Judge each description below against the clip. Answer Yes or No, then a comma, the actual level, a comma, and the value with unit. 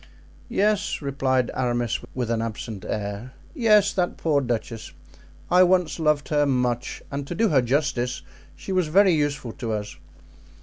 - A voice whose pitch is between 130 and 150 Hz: Yes, medium, 140 Hz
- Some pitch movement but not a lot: No, wide, 6.3 semitones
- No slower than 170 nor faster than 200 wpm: No, average, 155 wpm